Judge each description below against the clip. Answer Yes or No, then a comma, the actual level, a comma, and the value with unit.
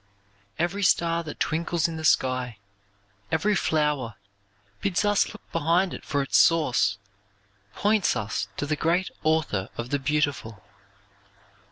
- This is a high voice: No, medium, 155 Hz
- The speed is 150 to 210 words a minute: No, slow, 135 wpm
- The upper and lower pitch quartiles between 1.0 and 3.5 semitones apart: No, average, 4.4 semitones